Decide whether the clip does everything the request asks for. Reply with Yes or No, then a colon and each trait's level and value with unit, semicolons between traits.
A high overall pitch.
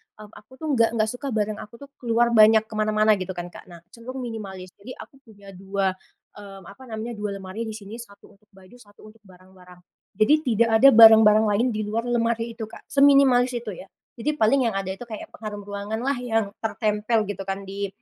Yes: high, 215 Hz